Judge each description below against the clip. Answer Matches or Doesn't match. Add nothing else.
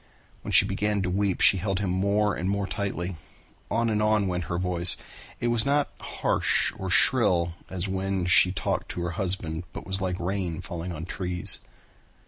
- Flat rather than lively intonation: Matches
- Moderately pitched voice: Doesn't match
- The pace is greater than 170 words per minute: Matches